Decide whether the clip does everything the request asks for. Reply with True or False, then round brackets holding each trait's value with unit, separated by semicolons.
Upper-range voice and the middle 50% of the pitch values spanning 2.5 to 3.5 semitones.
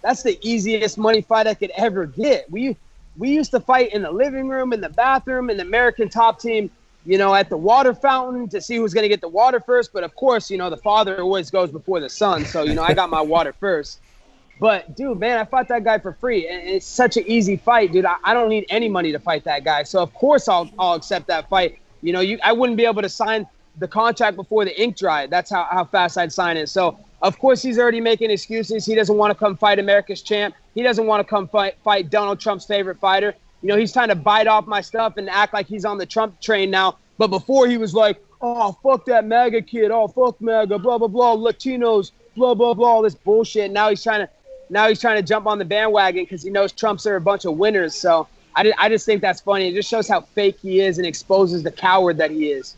True (210 Hz; 3.2 semitones)